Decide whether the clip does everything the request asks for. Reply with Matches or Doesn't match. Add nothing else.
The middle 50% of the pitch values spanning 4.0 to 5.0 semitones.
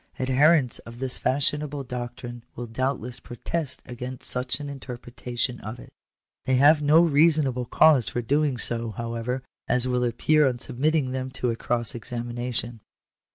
Doesn't match